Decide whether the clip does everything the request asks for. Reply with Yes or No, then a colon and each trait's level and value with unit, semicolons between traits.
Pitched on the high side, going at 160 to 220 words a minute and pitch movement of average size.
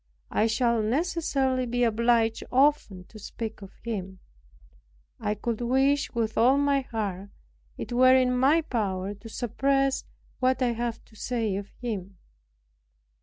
No: high, 235 Hz; average, 140 wpm; average, 3.3 semitones